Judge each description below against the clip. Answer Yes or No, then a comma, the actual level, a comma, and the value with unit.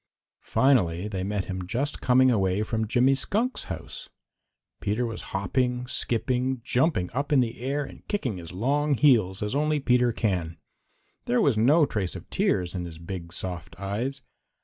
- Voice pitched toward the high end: No, low, 120 Hz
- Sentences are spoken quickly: No, average, 165 wpm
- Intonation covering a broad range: Yes, wide, 5.8 semitones